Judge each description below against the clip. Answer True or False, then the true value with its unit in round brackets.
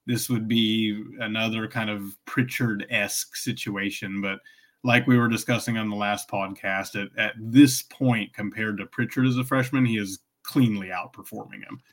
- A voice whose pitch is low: True (110 Hz)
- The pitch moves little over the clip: False (3.3 semitones)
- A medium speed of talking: True (165 wpm)